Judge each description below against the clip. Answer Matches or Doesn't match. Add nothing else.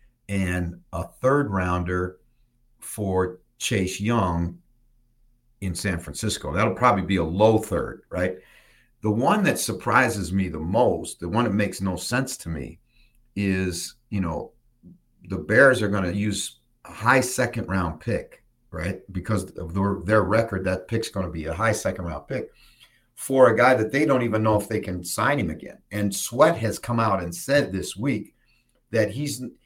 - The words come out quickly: Doesn't match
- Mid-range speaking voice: Doesn't match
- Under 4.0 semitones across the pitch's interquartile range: Doesn't match